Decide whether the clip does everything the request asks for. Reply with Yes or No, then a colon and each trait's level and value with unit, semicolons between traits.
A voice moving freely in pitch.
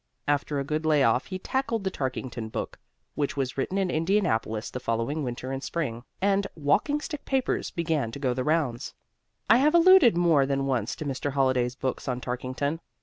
Yes: wide, 6.1 semitones